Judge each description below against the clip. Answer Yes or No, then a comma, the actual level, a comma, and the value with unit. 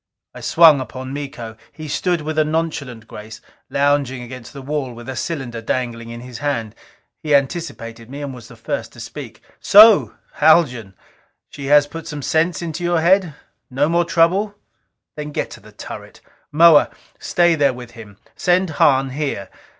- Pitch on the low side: No, medium, 145 Hz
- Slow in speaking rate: No, average, 165 wpm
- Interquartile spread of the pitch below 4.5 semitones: No, average, 4.9 semitones